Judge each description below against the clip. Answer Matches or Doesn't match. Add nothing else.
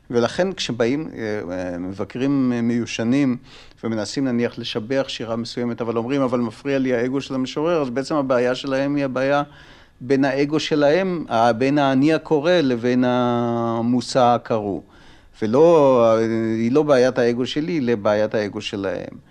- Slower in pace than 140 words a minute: Matches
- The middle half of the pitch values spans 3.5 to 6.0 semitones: Doesn't match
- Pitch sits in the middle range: Doesn't match